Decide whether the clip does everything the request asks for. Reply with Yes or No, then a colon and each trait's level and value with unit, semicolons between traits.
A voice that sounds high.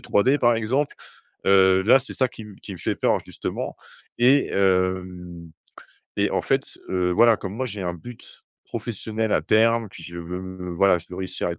No: very low, 95 Hz